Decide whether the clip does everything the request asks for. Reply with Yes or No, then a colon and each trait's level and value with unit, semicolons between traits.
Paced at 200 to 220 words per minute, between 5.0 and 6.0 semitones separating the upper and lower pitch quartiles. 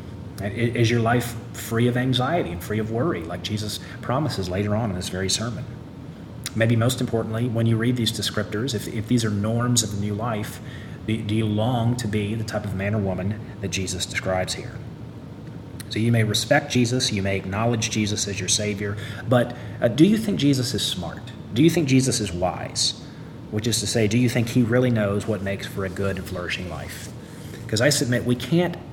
No: fast, 205 wpm; average, 3.0 semitones